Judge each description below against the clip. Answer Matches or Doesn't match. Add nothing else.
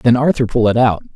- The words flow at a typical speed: Doesn't match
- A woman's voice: Doesn't match